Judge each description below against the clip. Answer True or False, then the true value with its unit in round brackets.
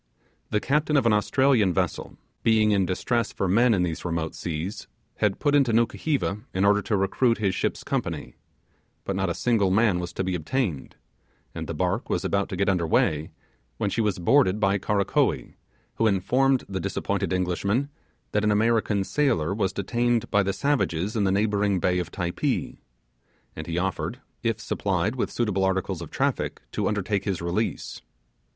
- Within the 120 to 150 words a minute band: False (175 wpm)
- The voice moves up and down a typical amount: True (3.6 semitones)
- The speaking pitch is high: False (100 Hz)